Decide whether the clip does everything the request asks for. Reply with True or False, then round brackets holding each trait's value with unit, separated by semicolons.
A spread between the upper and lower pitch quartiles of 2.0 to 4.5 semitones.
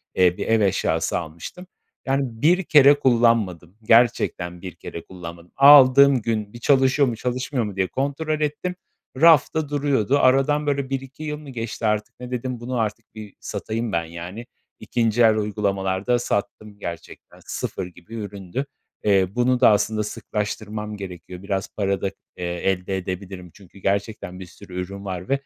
False (5.5 semitones)